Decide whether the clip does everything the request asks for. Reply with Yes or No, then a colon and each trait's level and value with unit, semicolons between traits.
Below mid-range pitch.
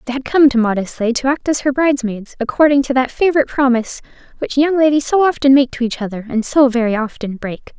No: very high, 260 Hz